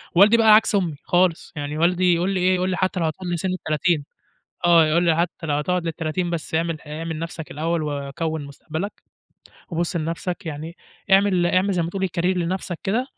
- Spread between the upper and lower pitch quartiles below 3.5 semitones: Yes, narrow, 2.5 semitones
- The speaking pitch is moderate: Yes, medium, 170 Hz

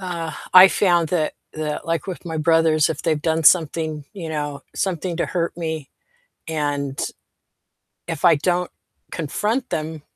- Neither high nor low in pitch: Yes, medium, 160 Hz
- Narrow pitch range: Yes, narrow, 2.3 semitones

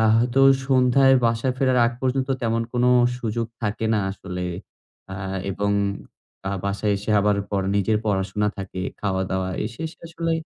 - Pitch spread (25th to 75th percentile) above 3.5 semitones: Yes, average, 4.2 semitones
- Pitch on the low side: Yes, low, 110 Hz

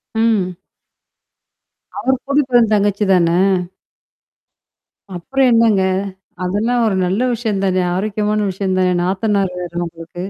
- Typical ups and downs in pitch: Yes, average, 3.7 semitones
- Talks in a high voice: Yes, high, 205 Hz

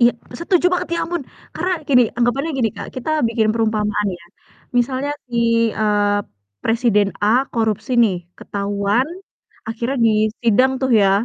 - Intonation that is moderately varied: Yes, average, 3.8 semitones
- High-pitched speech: Yes, high, 230 Hz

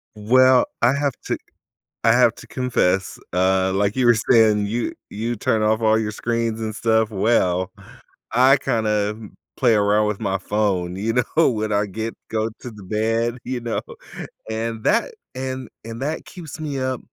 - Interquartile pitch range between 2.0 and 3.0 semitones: Yes, narrow, 2.6 semitones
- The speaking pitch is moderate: No, low, 110 Hz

